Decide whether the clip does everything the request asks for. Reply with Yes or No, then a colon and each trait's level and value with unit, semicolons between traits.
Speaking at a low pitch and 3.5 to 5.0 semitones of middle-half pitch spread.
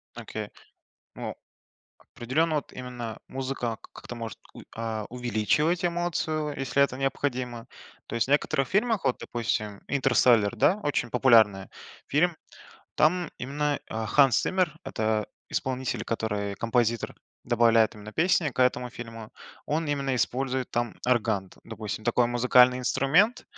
Yes: low, 125 Hz; average, 4.0 semitones